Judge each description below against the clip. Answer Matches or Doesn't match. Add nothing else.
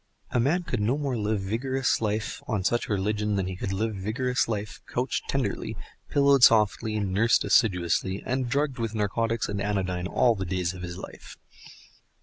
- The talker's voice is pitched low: Matches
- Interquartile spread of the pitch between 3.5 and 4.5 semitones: Matches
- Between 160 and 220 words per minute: Matches